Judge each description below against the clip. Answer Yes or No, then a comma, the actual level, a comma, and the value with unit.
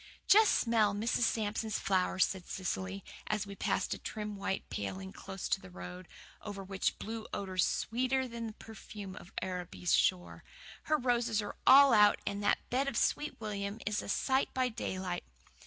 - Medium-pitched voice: No, high, 205 Hz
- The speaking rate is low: No, average, 170 wpm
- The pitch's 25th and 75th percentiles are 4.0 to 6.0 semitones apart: No, average, 3.6 semitones